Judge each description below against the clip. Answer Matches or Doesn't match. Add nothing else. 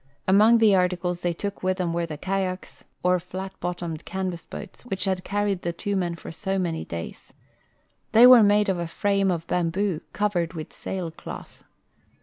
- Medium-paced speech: Matches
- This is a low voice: Doesn't match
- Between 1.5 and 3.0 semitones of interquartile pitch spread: Matches